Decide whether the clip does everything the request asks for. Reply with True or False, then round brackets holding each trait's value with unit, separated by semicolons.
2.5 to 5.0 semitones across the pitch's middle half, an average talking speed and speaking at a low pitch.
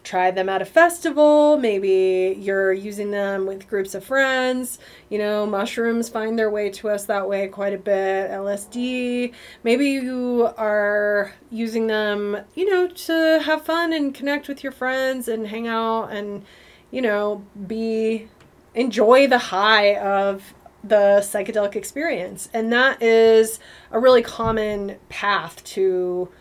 False (3.8 semitones; 145 wpm; 220 Hz)